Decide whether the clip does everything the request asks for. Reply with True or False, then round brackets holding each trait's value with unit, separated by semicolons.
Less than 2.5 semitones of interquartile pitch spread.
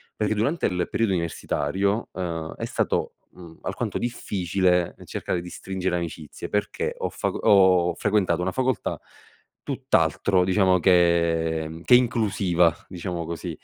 False (2.8 semitones)